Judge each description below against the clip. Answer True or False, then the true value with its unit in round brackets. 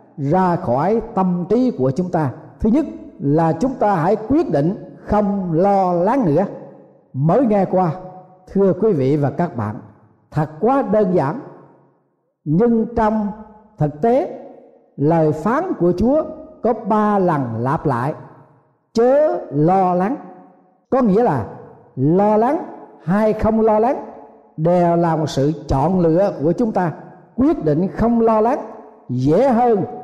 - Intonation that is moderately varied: False (6.5 semitones)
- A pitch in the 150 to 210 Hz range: True (185 Hz)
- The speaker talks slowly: True (145 wpm)